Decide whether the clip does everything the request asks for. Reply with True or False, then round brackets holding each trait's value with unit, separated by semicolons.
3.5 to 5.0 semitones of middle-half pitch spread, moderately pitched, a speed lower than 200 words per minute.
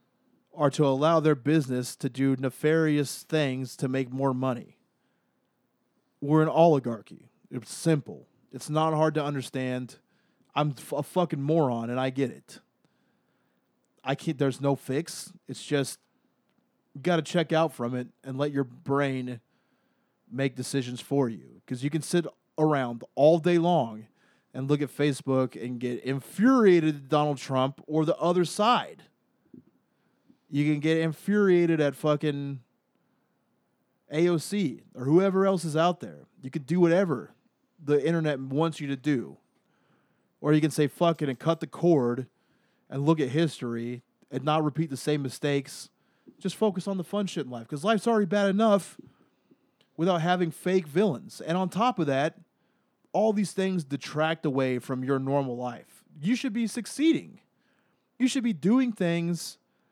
True (4.3 semitones; 150 Hz; 160 wpm)